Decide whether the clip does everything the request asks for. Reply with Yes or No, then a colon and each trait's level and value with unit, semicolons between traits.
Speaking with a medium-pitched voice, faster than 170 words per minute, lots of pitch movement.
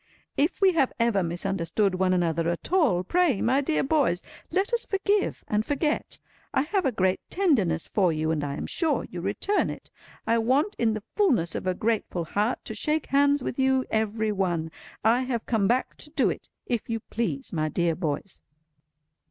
No: high, 225 Hz; average, 190 wpm; wide, 7.7 semitones